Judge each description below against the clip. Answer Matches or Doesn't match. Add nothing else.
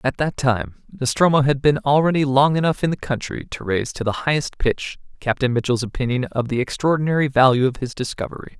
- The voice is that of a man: Matches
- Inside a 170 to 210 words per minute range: Matches